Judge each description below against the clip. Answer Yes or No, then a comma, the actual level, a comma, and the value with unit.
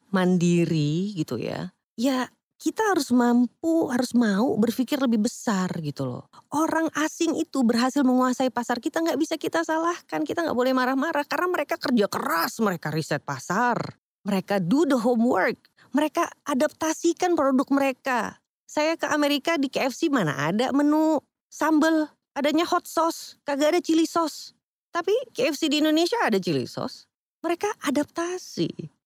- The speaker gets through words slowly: No, fast, 140 wpm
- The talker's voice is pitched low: No, very high, 280 Hz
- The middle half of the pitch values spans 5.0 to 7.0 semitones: Yes, wide, 5.6 semitones